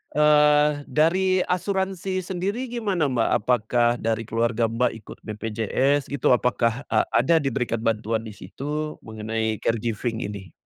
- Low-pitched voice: Yes, low, 125 Hz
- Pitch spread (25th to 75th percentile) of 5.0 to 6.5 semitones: Yes, average, 5.3 semitones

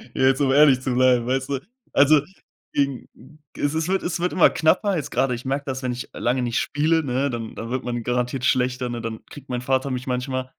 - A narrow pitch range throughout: Yes, narrow, 2.3 semitones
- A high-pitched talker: No, low, 130 Hz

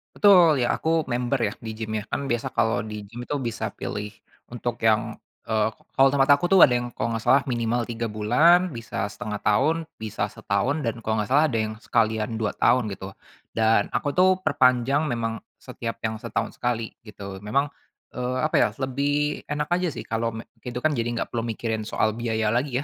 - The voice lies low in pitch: Yes, low, 120 Hz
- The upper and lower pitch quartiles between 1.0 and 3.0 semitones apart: No, average, 3.6 semitones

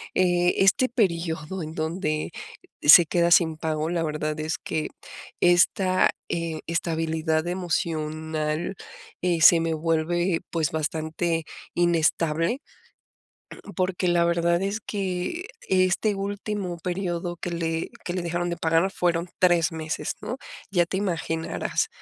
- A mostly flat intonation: Yes, narrow, 2.1 semitones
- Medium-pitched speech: Yes, medium, 170 Hz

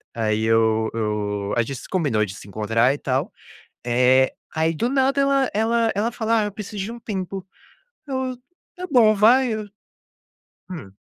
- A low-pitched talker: No, high, 190 Hz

